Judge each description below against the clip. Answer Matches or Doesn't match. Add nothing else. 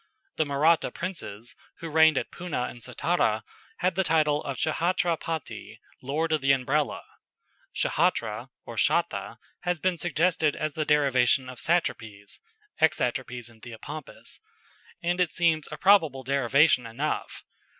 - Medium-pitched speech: Matches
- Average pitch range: Matches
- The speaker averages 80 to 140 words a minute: Matches